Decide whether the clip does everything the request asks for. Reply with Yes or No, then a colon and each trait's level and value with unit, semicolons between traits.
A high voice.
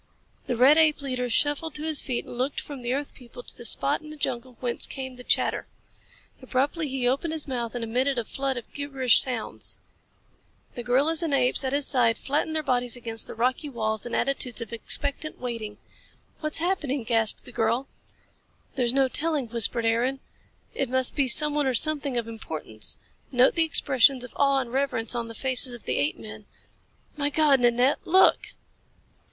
Yes: very high, 255 Hz